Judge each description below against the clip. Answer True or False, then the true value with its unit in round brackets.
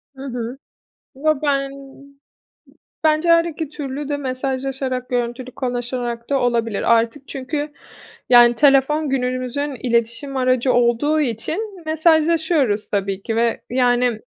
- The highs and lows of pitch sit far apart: False (3.4 semitones)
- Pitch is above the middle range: True (260 Hz)